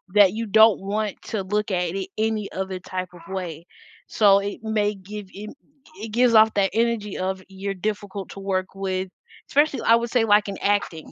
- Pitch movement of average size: No, narrow, 2.3 semitones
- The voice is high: Yes, high, 200 Hz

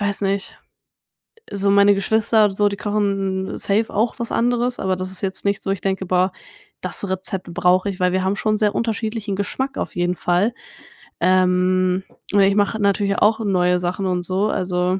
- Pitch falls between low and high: No, high, 195 Hz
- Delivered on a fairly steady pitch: Yes, narrow, 2.0 semitones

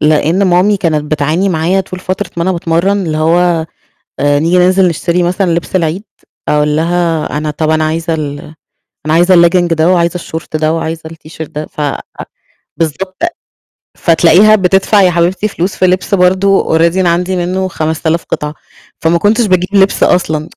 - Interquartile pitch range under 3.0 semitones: Yes, narrow, 2.6 semitones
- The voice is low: No, medium, 170 Hz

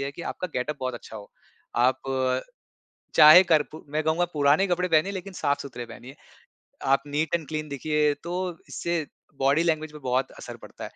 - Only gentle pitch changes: No, average, 3.1 semitones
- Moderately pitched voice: Yes, medium, 150 Hz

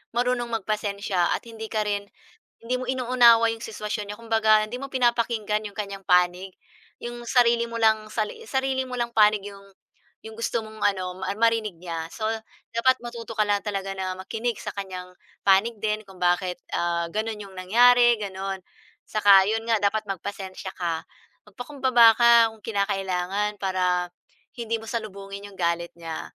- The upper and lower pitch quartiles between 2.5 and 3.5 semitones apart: Yes, average, 3.2 semitones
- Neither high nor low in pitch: No, high, 215 Hz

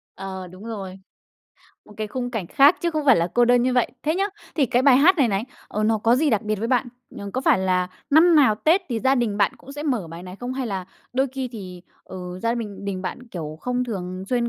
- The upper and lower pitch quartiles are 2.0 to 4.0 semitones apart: No, average, 5.2 semitones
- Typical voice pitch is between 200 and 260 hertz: Yes, high, 230 Hz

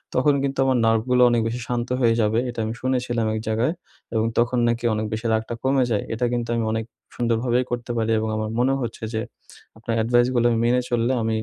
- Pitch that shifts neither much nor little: No, narrow, 1.8 semitones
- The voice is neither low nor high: No, low, 120 Hz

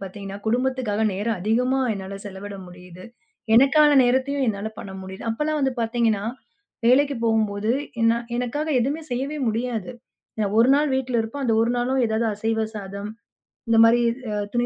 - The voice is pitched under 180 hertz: No, high, 230 Hz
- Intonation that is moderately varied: Yes, average, 4.0 semitones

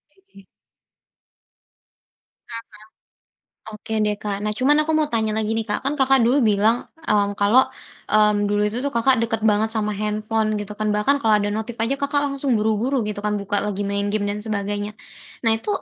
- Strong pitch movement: No, average, 2.8 semitones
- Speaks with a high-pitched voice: Yes, high, 215 Hz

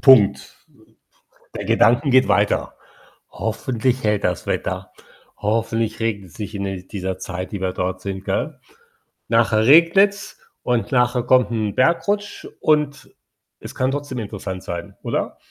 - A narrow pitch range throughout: No, average, 4.9 semitones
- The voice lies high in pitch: No, low, 115 Hz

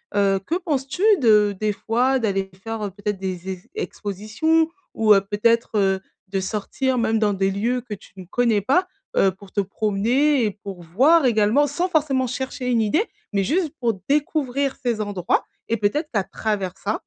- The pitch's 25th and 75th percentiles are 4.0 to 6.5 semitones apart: Yes, average, 4.9 semitones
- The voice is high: Yes, high, 220 Hz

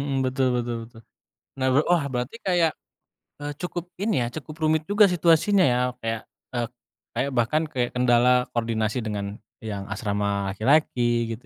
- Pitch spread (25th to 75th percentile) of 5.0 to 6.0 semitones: Yes, wide, 5.5 semitones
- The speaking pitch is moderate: No, low, 125 Hz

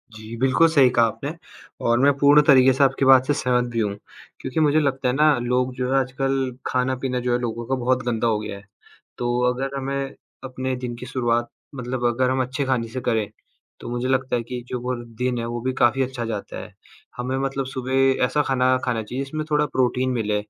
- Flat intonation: Yes, narrow, 1.7 semitones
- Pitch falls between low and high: No, low, 125 Hz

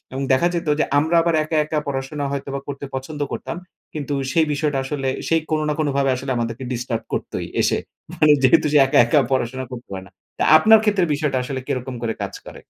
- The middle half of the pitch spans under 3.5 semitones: Yes, average, 2.8 semitones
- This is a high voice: No, medium, 140 Hz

